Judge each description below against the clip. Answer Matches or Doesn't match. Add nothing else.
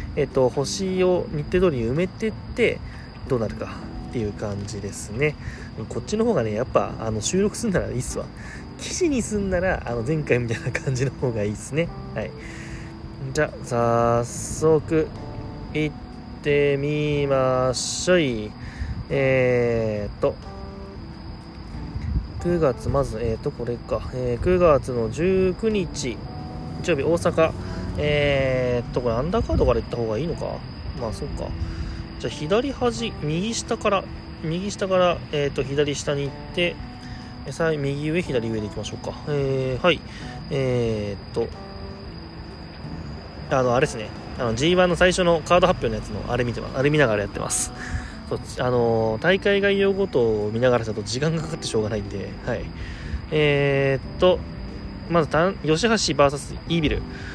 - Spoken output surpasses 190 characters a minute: Matches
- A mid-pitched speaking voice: Doesn't match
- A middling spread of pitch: Doesn't match